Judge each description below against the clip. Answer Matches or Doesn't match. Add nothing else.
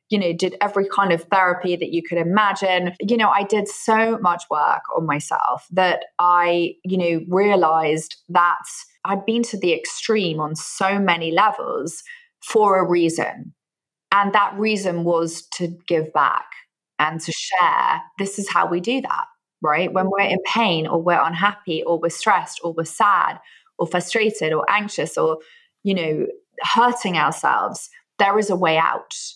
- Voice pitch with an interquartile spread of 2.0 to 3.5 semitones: Doesn't match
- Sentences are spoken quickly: Doesn't match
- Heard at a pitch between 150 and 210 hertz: Matches